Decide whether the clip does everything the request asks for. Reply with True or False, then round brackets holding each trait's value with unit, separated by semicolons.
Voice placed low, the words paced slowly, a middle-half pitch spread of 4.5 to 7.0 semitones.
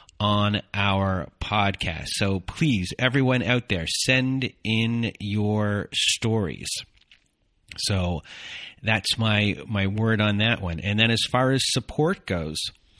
False (105 Hz; 125 wpm; 3.2 semitones)